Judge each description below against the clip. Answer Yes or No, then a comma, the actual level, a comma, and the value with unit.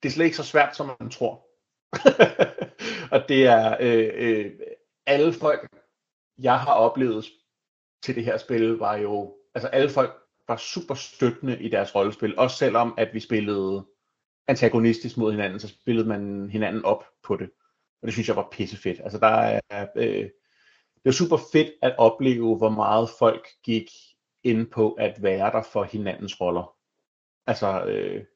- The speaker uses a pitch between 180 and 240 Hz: No, low, 115 Hz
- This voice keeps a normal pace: Yes, average, 170 wpm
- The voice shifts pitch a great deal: Yes, wide, 5.7 semitones